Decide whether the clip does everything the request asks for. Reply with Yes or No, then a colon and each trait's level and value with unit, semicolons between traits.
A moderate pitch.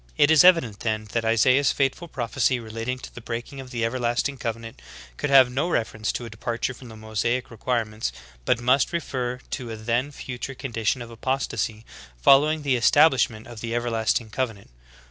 No: low, 120 Hz